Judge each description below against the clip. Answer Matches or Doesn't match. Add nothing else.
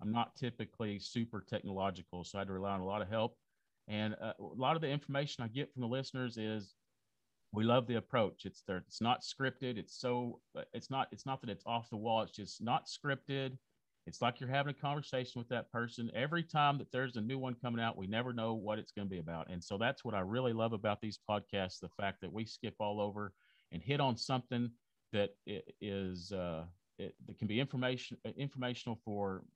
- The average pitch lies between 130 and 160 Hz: Doesn't match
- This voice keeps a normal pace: Doesn't match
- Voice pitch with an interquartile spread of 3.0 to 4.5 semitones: Matches